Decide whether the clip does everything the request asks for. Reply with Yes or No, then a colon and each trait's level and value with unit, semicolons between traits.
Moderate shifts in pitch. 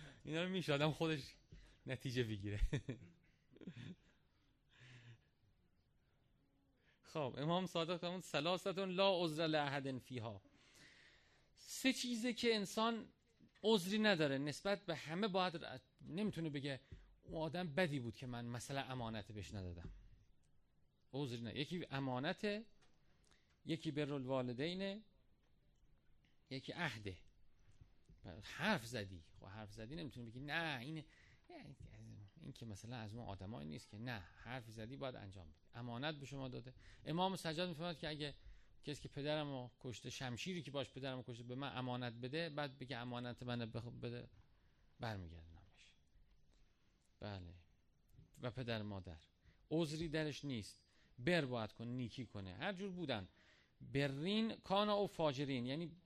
No: wide, 6.5 semitones